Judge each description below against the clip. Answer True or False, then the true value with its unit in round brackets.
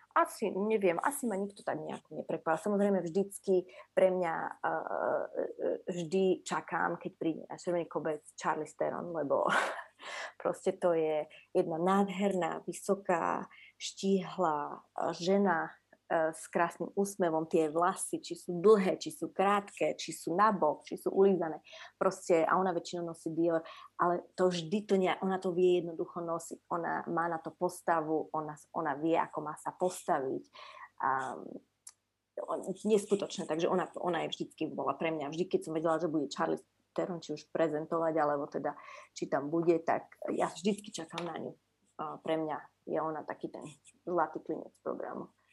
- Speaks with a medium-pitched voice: True (175 Hz)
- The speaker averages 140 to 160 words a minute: True (155 wpm)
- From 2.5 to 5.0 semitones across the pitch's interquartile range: True (2.9 semitones)